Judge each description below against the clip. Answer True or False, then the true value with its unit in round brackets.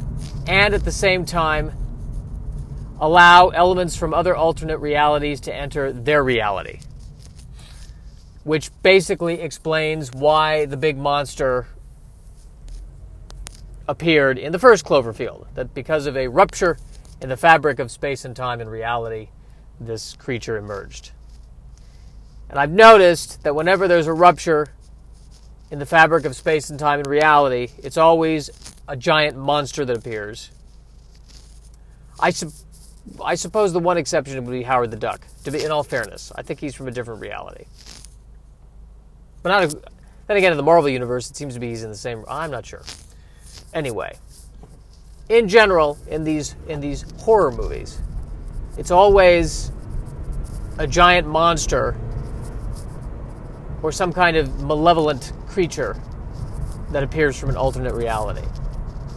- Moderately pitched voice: True (145 Hz)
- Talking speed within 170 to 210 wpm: False (140 wpm)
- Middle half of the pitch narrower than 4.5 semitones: False (5.1 semitones)